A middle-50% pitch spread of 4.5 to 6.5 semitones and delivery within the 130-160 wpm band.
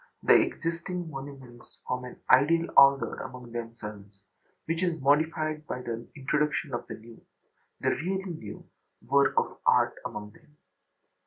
Yes: average, 5.1 semitones; average, 140 wpm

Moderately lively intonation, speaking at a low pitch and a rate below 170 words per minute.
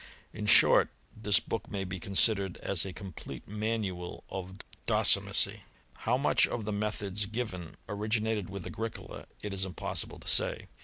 No: narrow, 2.3 semitones; low, 100 Hz; average, 155 wpm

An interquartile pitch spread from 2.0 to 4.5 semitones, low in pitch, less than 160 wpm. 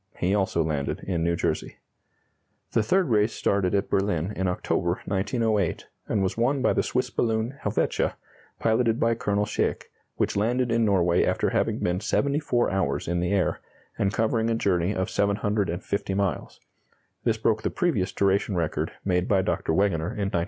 No: average, 3.6 semitones; low, 100 Hz; average, 170 wpm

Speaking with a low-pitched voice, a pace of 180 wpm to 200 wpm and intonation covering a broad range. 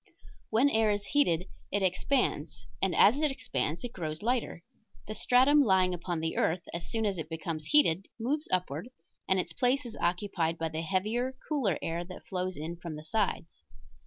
No: medium, 185 Hz; average, 185 wpm; wide, 6.1 semitones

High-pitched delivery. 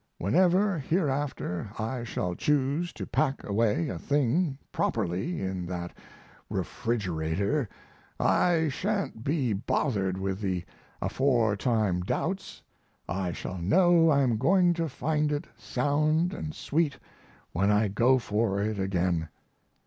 No: low, 120 Hz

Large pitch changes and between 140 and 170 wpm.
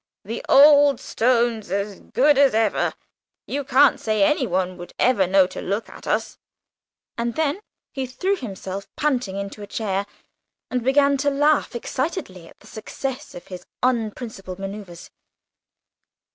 Yes: wide, 5.9 semitones; average, 145 wpm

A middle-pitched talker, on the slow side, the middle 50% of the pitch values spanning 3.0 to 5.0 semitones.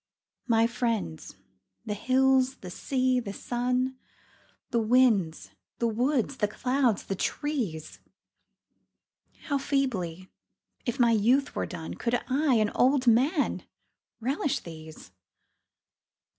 No: high, 240 Hz; slow, 110 wpm; average, 4.1 semitones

